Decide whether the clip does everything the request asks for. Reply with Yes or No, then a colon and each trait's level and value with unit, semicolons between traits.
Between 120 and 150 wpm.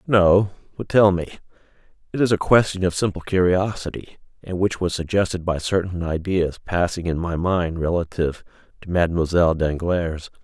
Yes: average, 145 wpm